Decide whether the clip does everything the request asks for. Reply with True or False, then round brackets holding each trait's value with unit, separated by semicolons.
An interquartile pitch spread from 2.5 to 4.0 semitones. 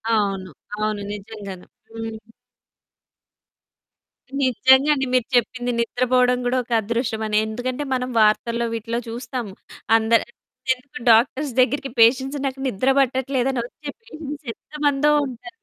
True (2.9 semitones)